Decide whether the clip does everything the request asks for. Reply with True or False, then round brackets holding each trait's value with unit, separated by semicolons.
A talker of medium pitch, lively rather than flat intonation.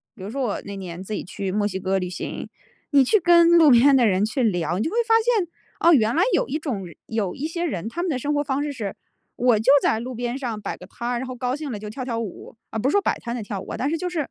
False (245 Hz; 5.9 semitones)